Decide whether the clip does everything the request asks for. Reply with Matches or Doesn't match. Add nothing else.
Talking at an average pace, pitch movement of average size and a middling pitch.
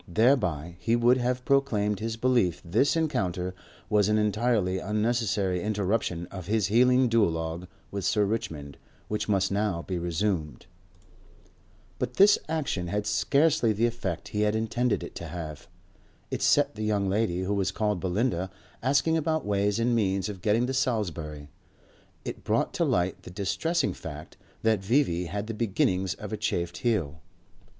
Doesn't match